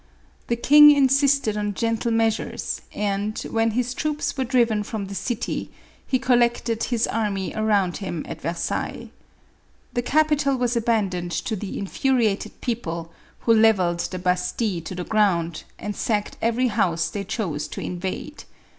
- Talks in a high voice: Yes, high, 220 Hz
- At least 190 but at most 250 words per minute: No, average, 150 wpm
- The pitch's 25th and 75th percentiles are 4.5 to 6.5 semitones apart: No, average, 4.1 semitones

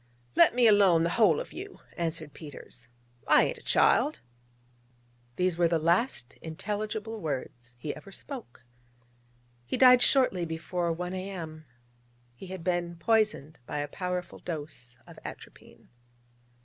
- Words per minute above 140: No, slow, 135 wpm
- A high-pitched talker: No, medium, 175 Hz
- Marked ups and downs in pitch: No, average, 4.8 semitones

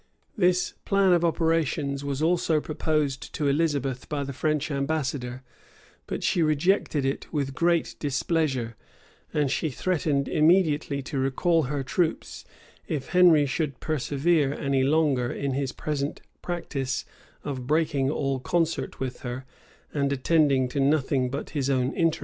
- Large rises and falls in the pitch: No, average, 3.1 semitones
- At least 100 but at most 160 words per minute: Yes, average, 140 wpm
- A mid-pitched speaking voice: Yes, medium, 145 Hz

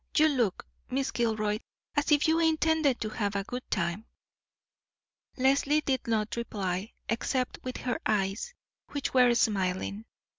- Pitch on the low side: No, high, 235 Hz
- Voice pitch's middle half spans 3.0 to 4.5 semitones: No, average, 5.0 semitones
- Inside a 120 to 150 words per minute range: Yes, average, 140 wpm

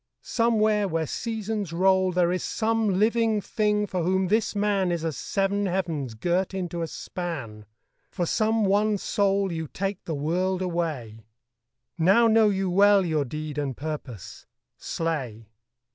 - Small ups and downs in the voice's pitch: No, average, 4.2 semitones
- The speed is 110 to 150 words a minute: Yes, average, 145 wpm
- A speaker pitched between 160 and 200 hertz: Yes, medium, 185 Hz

